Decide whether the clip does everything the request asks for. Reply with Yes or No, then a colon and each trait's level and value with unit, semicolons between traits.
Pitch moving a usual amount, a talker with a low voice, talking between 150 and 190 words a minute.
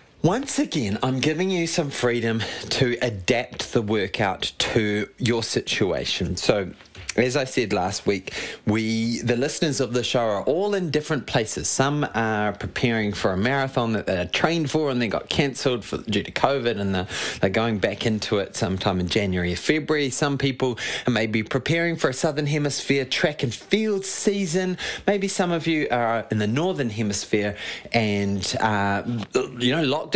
No: wide, 6.0 semitones; low, 120 Hz; average, 175 wpm